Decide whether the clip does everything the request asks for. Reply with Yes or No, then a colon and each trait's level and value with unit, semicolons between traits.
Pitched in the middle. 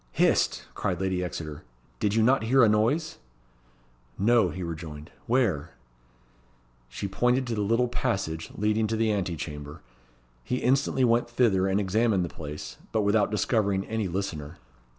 No: low, 105 Hz